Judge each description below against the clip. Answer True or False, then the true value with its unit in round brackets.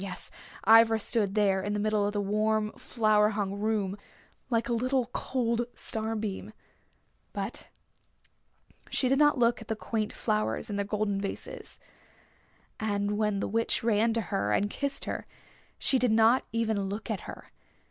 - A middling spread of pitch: False (2.0 semitones)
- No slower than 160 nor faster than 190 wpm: True (165 wpm)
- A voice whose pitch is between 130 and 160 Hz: False (215 Hz)